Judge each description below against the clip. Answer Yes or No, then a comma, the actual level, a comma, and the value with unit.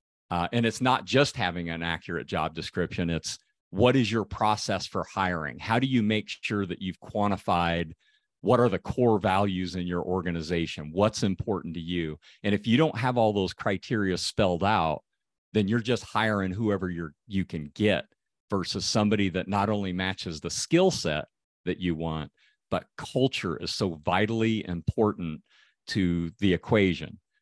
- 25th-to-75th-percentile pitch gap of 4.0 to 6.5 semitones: Yes, average, 4.3 semitones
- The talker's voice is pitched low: Yes, low, 100 Hz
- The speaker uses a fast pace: No, average, 170 wpm